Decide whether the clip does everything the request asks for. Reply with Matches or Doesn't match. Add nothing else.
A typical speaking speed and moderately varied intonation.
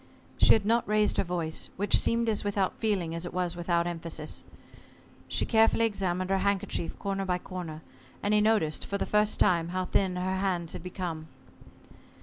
Matches